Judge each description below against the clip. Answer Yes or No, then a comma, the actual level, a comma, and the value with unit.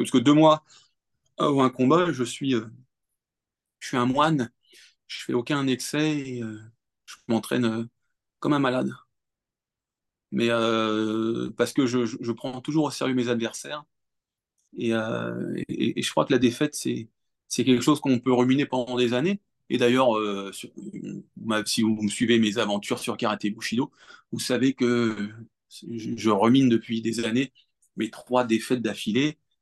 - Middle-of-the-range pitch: No, low, 120 Hz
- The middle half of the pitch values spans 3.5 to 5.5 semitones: No, narrow, 2.5 semitones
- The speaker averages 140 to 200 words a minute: Yes, average, 170 wpm